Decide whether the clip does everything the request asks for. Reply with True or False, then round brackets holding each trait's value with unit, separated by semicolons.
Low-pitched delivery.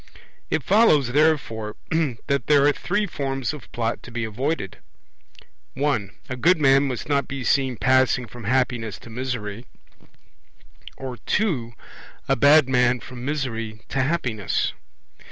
True (130 Hz)